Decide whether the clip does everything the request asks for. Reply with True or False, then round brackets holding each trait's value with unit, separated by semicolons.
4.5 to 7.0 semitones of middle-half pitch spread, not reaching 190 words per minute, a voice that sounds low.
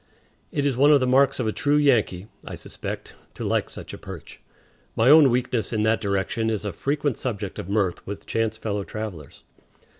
False (4.8 semitones; 200 wpm; 110 Hz)